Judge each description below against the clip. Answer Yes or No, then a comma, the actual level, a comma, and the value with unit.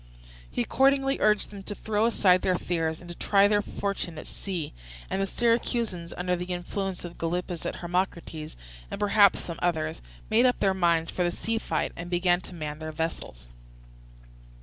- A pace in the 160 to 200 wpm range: Yes, average, 180 wpm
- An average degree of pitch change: Yes, average, 3.3 semitones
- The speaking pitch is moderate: Yes, medium, 180 Hz